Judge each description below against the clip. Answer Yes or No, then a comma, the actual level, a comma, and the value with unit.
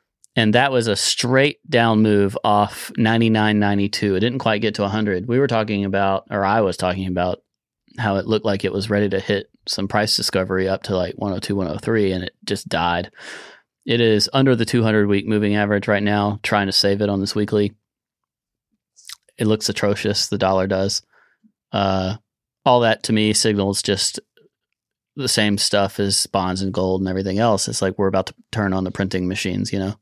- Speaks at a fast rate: No, average, 195 wpm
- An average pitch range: No, narrow, 2.0 semitones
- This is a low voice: Yes, low, 105 Hz